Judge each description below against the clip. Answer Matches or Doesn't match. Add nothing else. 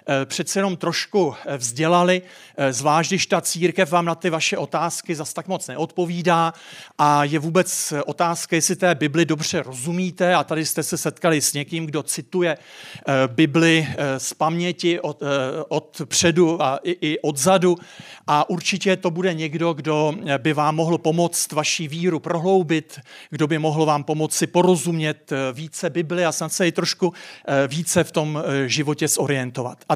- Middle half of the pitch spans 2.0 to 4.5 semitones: Matches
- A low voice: Doesn't match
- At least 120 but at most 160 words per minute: Matches